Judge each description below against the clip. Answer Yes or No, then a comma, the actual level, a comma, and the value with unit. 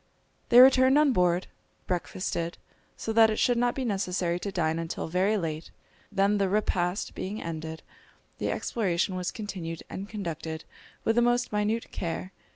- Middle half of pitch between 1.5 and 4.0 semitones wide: No, average, 4.5 semitones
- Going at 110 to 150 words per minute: No, average, 160 wpm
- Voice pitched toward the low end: No, high, 190 Hz